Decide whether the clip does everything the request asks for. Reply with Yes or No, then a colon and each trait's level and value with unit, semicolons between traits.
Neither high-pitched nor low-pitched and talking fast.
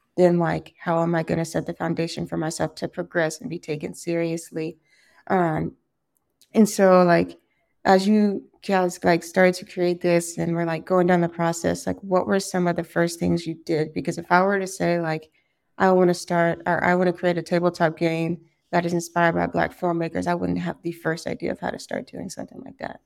Yes: medium, 170 Hz; fast, 225 wpm